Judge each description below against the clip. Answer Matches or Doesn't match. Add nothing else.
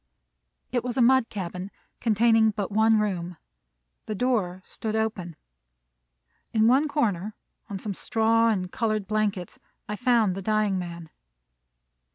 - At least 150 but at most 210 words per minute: Doesn't match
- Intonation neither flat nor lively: Matches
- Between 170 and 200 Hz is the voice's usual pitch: Doesn't match